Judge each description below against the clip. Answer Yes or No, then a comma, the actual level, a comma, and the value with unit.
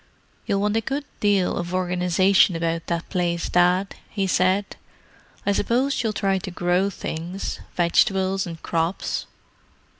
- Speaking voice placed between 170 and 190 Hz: Yes, medium, 185 Hz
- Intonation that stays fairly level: Yes, narrow, 2.3 semitones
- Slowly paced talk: Yes, slow, 130 wpm